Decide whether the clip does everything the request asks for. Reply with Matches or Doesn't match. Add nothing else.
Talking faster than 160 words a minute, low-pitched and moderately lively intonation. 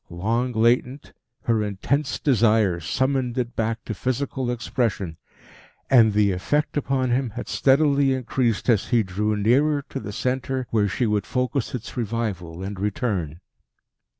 Doesn't match